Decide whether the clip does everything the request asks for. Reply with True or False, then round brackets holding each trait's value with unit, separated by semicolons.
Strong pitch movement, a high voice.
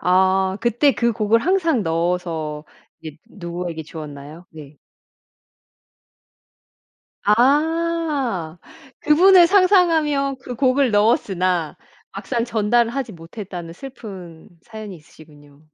True (8.5 semitones; 210 Hz)